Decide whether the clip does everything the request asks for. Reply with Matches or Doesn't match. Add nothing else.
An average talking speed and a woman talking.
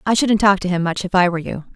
Doesn't match